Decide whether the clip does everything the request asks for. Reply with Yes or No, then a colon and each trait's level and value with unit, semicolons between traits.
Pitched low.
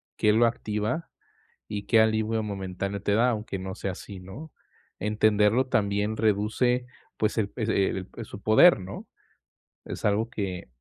Yes: low, 105 Hz